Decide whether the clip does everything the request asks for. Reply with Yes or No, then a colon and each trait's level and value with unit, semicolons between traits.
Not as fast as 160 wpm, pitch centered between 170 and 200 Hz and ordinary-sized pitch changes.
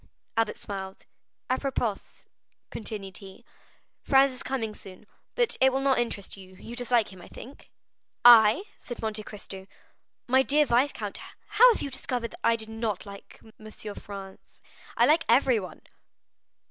No: average, 145 wpm; high, 230 Hz; average, 4.7 semitones